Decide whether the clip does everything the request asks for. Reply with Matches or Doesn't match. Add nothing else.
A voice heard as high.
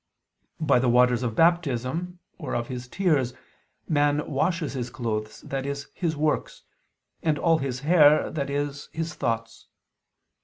Doesn't match